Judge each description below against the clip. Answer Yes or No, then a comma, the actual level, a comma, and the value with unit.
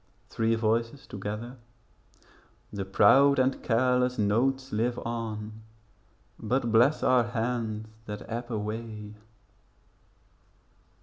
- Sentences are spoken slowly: Yes, slow, 95 wpm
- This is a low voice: Yes, low, 115 Hz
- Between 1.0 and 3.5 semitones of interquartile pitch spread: Yes, average, 2.7 semitones